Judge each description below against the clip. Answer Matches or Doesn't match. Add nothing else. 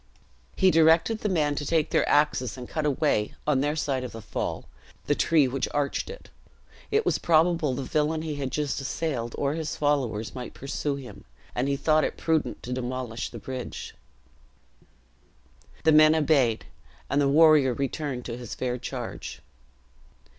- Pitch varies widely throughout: Doesn't match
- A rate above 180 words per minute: Doesn't match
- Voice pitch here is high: Doesn't match